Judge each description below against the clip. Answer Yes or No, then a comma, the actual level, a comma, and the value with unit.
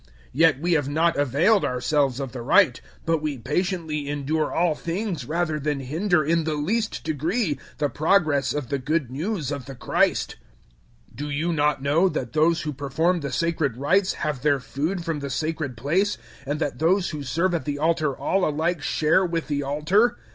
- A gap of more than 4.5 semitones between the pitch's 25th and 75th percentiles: No, average, 3.0 semitones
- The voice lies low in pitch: No, medium, 155 Hz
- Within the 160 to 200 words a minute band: Yes, average, 190 wpm